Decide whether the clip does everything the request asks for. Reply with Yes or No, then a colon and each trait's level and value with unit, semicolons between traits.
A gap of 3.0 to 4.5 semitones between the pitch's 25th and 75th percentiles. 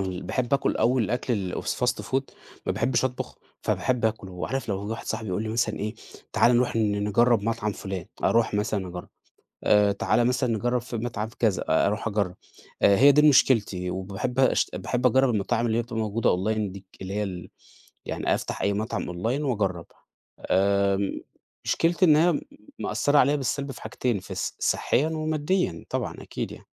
Yes: average, 4.1 semitones